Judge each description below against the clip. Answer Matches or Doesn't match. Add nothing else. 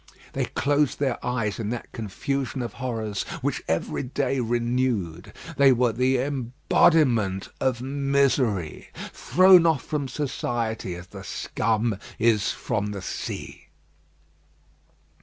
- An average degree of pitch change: Matches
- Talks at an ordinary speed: Doesn't match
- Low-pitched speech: Matches